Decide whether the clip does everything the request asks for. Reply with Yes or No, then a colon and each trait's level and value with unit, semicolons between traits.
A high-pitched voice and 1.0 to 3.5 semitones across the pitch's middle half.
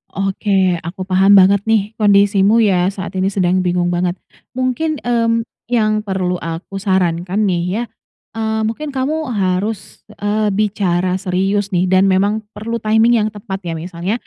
Yes: high, 195 Hz; average, 2.8 semitones